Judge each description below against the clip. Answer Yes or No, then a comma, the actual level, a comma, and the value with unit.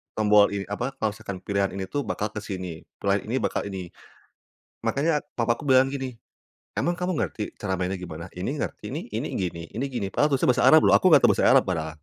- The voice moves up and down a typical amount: No, wide, 5.8 semitones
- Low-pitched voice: Yes, low, 105 Hz